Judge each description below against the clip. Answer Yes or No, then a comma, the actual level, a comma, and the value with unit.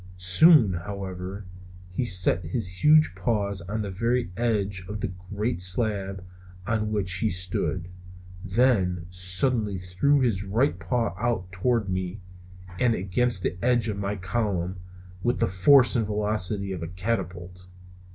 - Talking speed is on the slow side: No, average, 145 wpm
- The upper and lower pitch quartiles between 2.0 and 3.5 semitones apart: No, average, 4.0 semitones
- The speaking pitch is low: Yes, low, 100 Hz